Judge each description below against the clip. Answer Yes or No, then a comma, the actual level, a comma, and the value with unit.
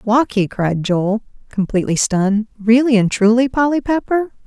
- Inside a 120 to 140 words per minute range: Yes, slow, 135 wpm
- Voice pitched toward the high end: Yes, high, 225 Hz